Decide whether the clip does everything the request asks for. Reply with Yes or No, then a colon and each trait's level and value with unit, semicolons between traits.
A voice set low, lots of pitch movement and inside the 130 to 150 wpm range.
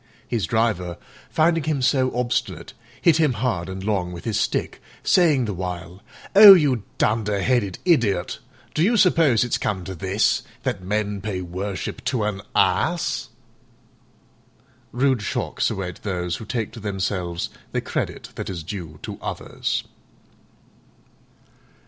Yes: low, 105 Hz; wide, 5.7 semitones; average, 140 wpm